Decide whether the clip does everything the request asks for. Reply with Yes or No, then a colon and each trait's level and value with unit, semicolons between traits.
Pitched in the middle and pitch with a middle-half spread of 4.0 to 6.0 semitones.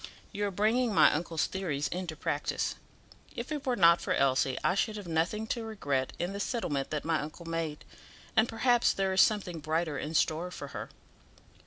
Yes: medium, 175 Hz; average, 5.3 semitones